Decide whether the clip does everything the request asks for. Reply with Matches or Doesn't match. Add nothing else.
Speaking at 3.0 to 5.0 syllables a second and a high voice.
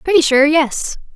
Matches